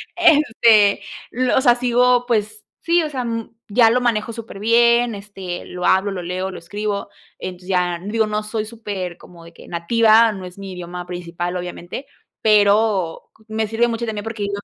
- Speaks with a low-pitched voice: No, high, 210 Hz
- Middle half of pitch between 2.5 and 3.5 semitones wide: No, average, 4.0 semitones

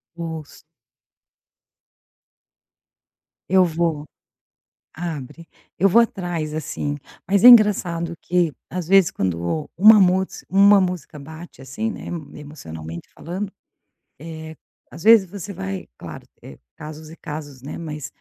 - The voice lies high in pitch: No, medium, 170 Hz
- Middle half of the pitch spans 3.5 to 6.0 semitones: Yes, average, 4.1 semitones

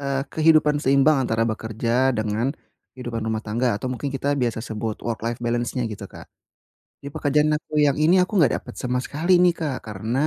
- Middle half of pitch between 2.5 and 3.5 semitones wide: No, average, 4.5 semitones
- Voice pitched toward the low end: Yes, low, 125 Hz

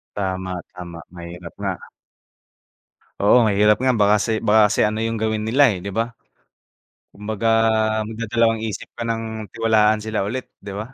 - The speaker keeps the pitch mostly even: Yes, narrow, 2.1 semitones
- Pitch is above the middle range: No, low, 110 Hz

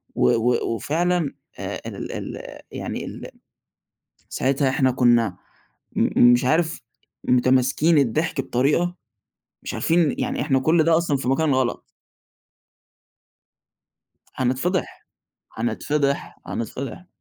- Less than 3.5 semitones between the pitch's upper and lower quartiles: No, average, 4.4 semitones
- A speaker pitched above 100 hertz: Yes, low, 135 Hz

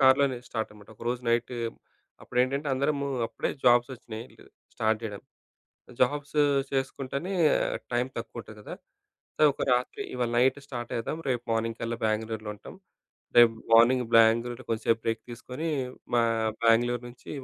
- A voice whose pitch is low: Yes, low, 120 Hz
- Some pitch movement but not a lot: No, narrow, 2.3 semitones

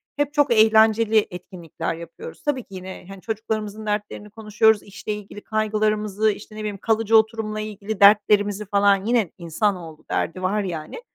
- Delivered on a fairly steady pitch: Yes, narrow, 1.9 semitones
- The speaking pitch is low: No, high, 210 Hz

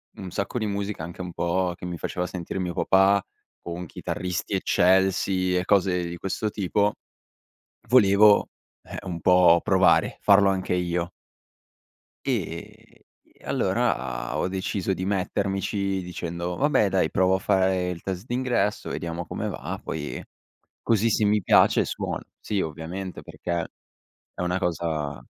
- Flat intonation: Yes, narrow, 2.1 semitones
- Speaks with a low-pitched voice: Yes, very low, 95 Hz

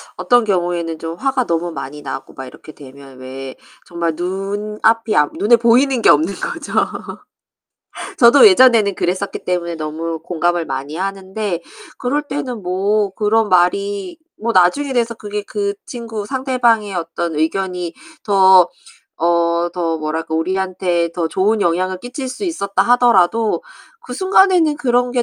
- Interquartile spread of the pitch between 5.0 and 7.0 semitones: Yes, wide, 5.4 semitones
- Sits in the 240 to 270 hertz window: No, high, 190 Hz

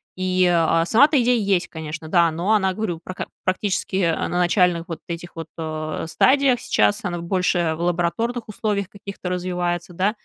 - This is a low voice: No, medium, 180 Hz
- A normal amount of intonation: Yes, average, 3.0 semitones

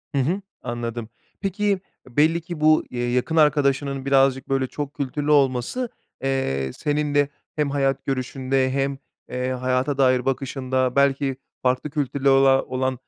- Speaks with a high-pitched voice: No, low, 135 Hz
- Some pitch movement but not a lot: No, narrow, 2.1 semitones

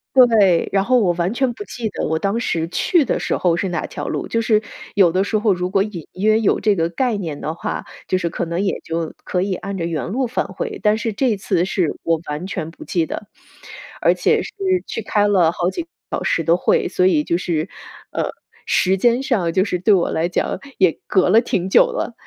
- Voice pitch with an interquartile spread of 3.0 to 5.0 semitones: Yes, average, 4.2 semitones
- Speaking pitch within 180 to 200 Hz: Yes, high, 190 Hz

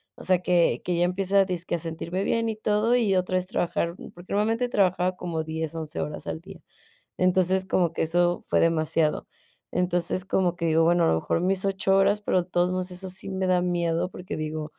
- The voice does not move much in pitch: Yes, narrow, 2.1 semitones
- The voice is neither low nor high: Yes, medium, 180 Hz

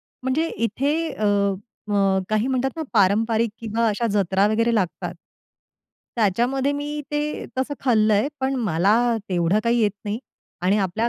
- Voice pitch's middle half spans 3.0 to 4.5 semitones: Yes, average, 4.2 semitones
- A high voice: Yes, high, 225 Hz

